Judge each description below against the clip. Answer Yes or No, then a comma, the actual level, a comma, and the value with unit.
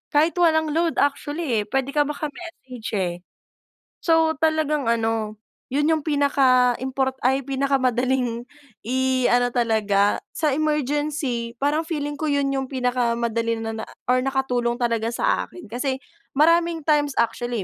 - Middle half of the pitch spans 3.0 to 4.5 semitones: Yes, average, 3.8 semitones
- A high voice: Yes, very high, 265 Hz